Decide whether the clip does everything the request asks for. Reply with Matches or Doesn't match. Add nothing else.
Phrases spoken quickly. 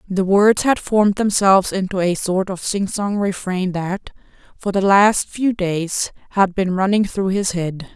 Doesn't match